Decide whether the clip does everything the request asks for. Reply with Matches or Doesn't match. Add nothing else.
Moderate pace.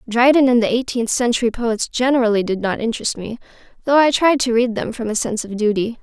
Doesn't match